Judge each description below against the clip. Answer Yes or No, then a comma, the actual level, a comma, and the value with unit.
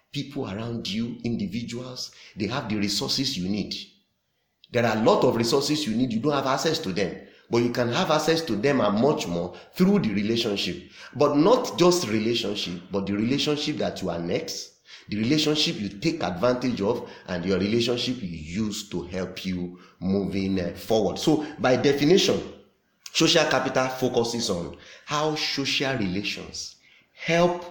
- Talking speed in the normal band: Yes, average, 160 wpm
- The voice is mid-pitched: No, low, 120 Hz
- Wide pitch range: Yes, wide, 7.0 semitones